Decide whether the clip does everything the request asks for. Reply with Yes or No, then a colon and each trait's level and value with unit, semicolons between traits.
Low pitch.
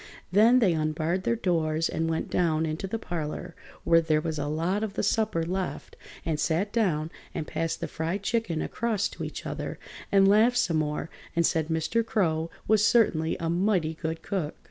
No: medium, 170 Hz